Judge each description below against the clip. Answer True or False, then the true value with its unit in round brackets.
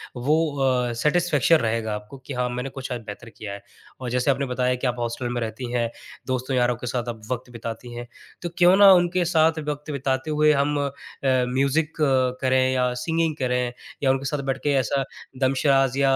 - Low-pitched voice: True (130 Hz)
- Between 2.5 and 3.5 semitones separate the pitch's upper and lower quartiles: True (2.9 semitones)